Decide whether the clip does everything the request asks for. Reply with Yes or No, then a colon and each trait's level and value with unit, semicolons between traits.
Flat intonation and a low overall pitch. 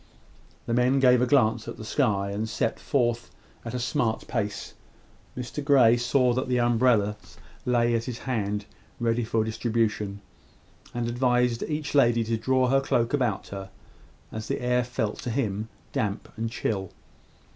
Yes: narrow, 2.3 semitones; low, 120 Hz